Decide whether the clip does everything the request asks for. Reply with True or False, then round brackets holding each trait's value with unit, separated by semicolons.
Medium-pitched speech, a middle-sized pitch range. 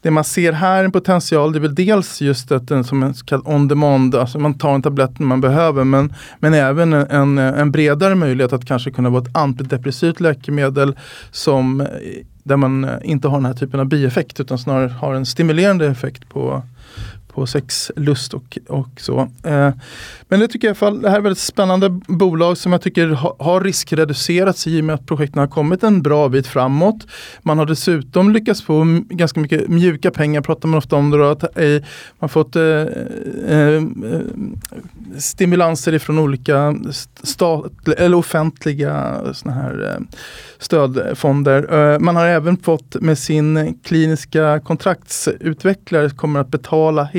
True (150 Hz; 3.4 semitones)